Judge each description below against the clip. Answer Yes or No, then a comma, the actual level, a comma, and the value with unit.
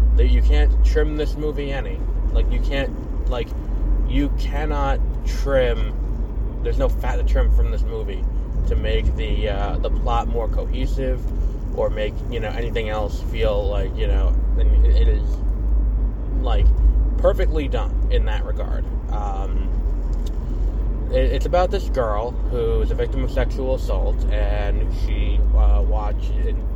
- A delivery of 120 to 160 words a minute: Yes, average, 150 wpm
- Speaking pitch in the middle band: No, very low, 85 Hz